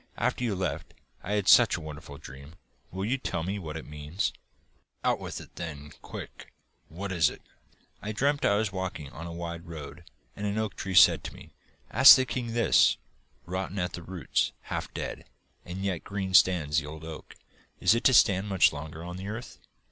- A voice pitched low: Yes, very low, 90 Hz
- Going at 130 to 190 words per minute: No, average, 200 wpm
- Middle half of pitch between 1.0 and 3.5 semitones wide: No, average, 4.1 semitones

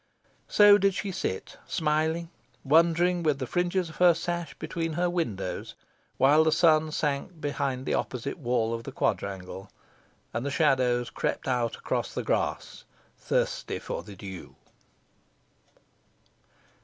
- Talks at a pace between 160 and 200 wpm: No, slow, 135 wpm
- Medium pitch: Yes, medium, 150 Hz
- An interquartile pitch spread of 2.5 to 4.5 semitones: No, wide, 5.6 semitones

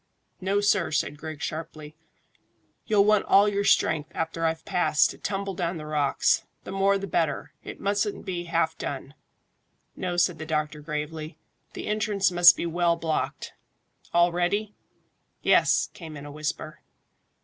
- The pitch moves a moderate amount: Yes, average, 4.0 semitones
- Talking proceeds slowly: No, average, 155 wpm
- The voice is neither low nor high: Yes, medium, 170 Hz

